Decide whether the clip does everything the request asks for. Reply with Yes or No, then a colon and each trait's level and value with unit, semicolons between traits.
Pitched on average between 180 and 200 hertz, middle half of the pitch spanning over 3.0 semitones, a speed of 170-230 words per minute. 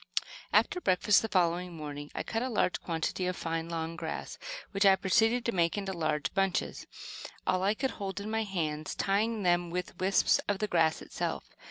Yes: medium, 185 Hz; average, 3.5 semitones; average, 195 wpm